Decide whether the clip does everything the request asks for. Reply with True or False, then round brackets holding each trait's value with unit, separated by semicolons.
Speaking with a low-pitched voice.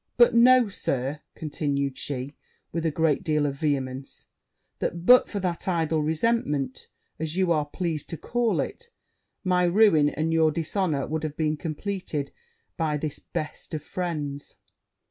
False (160 Hz)